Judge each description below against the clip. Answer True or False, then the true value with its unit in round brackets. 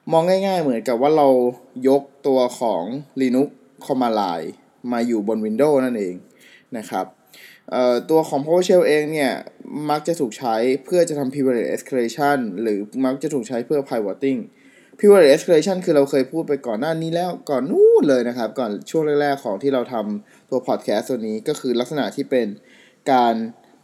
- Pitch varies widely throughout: False (4.0 semitones)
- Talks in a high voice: False (135 Hz)